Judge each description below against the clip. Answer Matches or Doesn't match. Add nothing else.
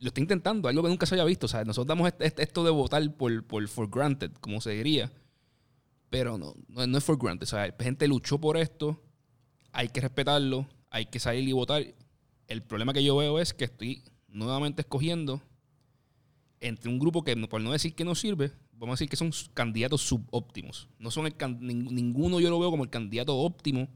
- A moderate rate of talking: Doesn't match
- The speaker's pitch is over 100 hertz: Matches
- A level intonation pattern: Doesn't match